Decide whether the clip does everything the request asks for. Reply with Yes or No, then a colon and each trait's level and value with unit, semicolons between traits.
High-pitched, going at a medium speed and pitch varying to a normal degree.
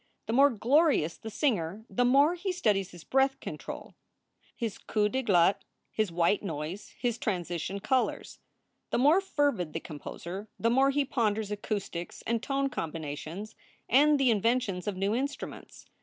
No: high, 220 Hz; average, 155 wpm; wide, 6.5 semitones